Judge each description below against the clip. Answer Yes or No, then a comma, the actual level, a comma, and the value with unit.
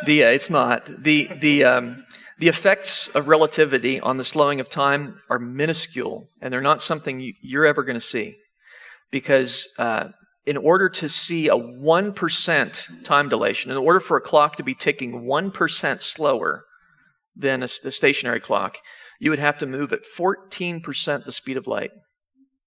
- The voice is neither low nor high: Yes, medium, 150 Hz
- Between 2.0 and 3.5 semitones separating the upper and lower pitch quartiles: No, average, 4.0 semitones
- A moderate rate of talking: Yes, average, 165 wpm